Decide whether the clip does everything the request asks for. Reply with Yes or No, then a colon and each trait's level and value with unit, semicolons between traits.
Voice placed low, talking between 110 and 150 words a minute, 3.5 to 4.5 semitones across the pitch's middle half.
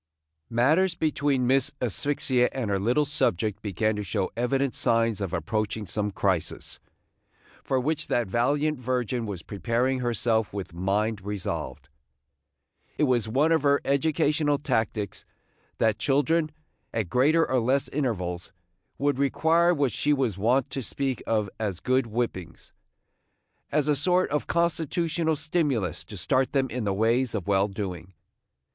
No: low, 125 Hz; average, 145 wpm; wide, 5.5 semitones